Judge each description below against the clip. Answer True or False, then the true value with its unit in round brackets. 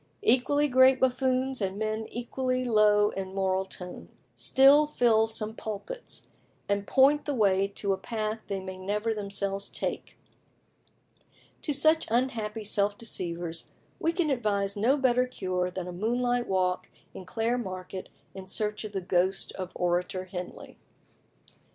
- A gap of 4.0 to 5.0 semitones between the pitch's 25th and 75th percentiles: True (4.7 semitones)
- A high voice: True (210 Hz)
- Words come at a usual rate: True (145 wpm)